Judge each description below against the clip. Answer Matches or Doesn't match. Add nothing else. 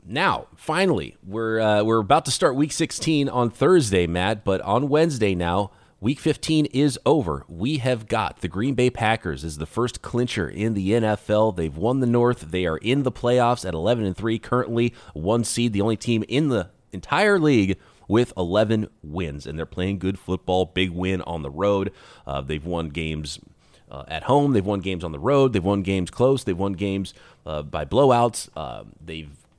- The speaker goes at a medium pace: Matches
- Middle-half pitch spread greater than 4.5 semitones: Matches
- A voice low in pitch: Matches